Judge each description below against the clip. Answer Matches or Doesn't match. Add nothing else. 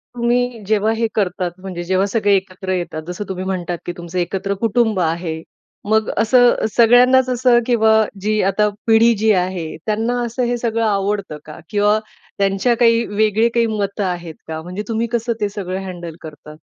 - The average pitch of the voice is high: Matches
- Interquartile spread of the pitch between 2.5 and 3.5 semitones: Doesn't match